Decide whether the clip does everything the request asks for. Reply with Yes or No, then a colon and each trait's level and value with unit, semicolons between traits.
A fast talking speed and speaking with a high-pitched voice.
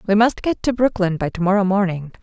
Yes: fast, 215 wpm; high, 200 Hz